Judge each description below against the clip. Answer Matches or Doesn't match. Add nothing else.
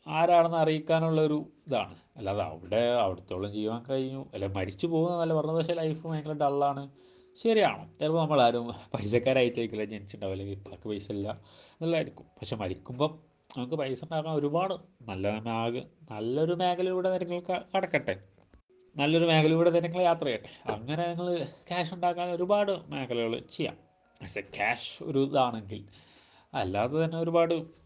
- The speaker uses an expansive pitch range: Matches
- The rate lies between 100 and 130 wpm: Matches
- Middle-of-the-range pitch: Matches